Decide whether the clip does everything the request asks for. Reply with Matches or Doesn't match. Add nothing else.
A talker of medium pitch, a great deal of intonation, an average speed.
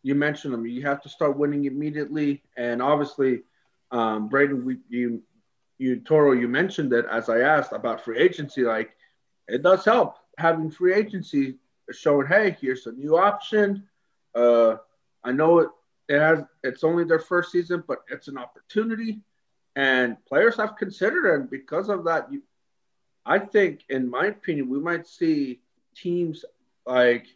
Matches